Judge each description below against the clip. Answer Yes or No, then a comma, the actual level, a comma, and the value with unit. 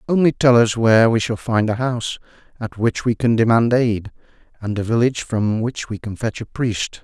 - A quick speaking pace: Yes, fast, 215 wpm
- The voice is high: No, low, 115 Hz